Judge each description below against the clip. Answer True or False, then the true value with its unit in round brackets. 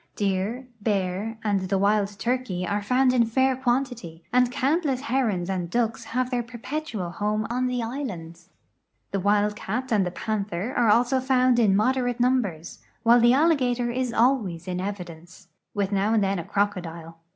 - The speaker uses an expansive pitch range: False (4.6 semitones)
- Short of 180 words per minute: True (165 wpm)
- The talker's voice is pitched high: True (220 Hz)